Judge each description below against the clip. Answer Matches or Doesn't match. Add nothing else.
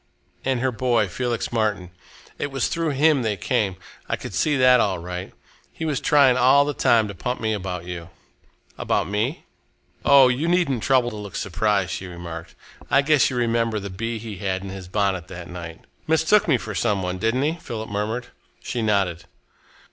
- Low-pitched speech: Matches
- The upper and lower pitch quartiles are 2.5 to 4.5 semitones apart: Doesn't match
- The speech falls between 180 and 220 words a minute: Matches